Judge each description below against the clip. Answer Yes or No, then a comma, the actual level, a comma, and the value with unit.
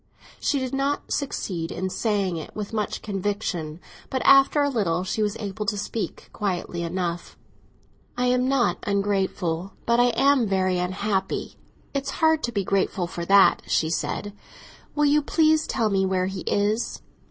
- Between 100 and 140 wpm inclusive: No, average, 165 wpm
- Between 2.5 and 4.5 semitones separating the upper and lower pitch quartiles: No, average, 5.1 semitones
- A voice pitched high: Yes, high, 205 Hz